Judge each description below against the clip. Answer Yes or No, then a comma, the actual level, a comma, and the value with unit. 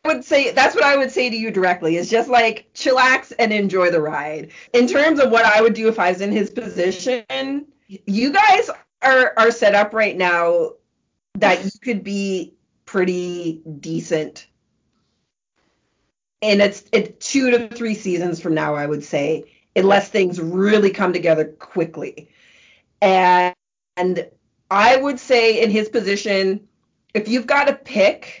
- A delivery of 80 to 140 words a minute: No, average, 165 wpm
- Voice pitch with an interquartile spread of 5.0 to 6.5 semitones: Yes, wide, 5.5 semitones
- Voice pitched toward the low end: No, high, 210 Hz